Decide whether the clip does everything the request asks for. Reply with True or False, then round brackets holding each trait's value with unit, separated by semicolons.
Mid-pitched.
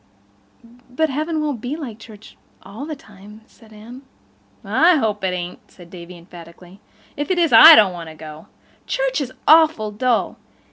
False (220 Hz)